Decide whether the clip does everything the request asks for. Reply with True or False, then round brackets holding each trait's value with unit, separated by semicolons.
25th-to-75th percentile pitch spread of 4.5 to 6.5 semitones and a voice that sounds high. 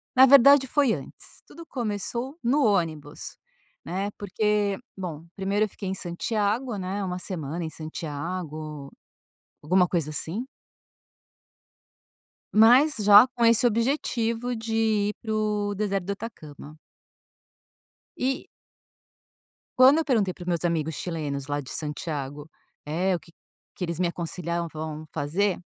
True (5.6 semitones; 195 Hz)